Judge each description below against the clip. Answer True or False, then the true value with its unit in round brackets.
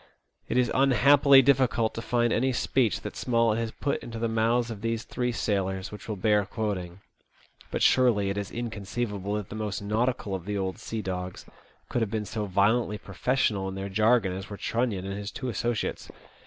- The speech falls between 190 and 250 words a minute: True (195 wpm)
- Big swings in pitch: False (3.2 semitones)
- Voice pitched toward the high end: False (110 Hz)